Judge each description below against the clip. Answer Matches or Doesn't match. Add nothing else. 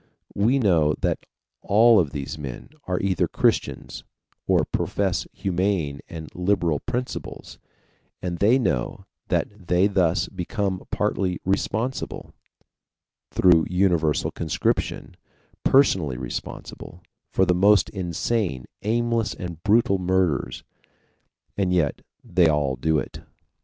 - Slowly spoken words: Matches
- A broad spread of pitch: Doesn't match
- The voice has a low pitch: Matches